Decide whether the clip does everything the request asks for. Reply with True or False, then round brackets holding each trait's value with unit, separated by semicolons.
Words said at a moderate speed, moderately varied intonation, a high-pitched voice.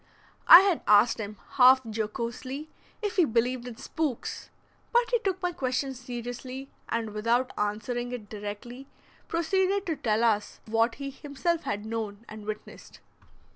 True (145 wpm; 4.8 semitones; 245 Hz)